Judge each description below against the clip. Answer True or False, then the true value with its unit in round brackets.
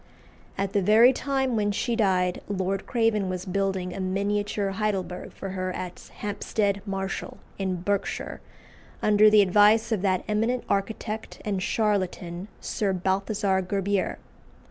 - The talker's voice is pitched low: False (200 Hz)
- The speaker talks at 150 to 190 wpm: False (135 wpm)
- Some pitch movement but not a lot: False (2.0 semitones)